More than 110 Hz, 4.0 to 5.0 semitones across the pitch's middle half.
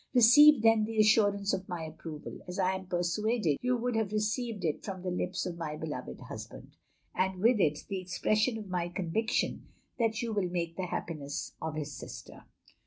Yes: high, 190 Hz; average, 4.6 semitones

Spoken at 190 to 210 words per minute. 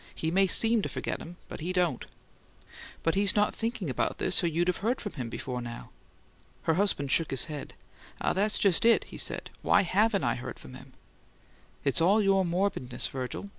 Yes: average, 200 wpm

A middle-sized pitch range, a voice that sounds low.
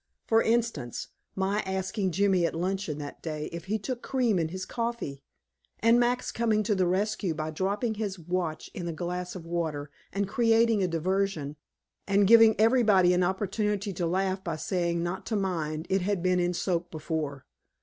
No: average, 3.7 semitones; high, 190 Hz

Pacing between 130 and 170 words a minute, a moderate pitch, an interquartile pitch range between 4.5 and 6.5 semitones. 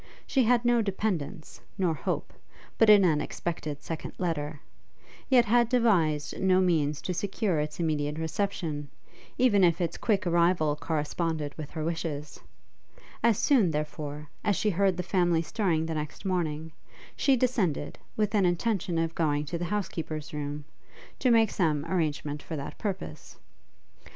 Yes: average, 150 wpm; medium, 170 Hz; average, 4.8 semitones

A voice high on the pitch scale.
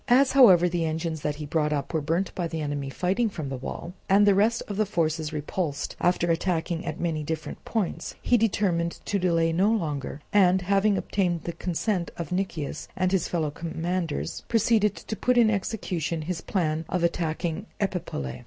No: medium, 175 Hz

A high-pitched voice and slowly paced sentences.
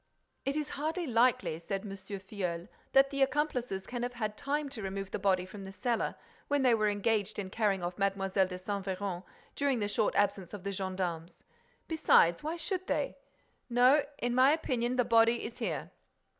No: high, 215 Hz; average, 180 wpm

